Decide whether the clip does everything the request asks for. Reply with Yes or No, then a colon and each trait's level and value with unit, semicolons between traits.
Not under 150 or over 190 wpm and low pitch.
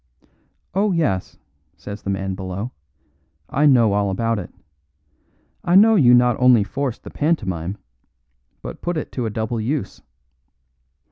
No: average, 140 wpm; low, 115 Hz